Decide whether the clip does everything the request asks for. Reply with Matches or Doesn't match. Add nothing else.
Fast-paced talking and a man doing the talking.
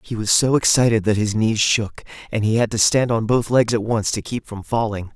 Matches